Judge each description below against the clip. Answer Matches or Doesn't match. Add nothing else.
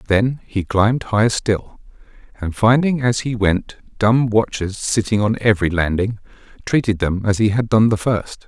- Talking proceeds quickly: Doesn't match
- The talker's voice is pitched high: Doesn't match